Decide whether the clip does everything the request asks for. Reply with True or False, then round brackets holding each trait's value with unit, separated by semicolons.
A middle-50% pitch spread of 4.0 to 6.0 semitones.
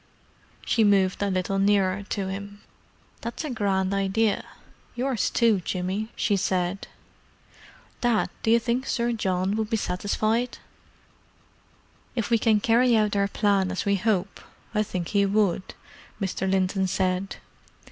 False (2.7 semitones)